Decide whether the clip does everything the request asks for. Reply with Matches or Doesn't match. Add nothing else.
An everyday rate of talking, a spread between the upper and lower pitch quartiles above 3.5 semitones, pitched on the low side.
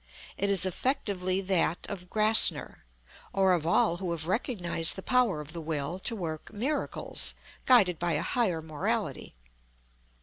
Doesn't match